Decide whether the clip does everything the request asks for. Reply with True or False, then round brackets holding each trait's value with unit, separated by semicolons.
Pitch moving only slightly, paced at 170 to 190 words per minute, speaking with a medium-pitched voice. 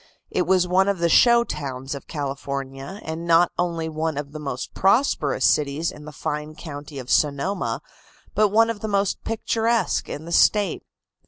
False (5.5 semitones; 175 wpm; 160 Hz)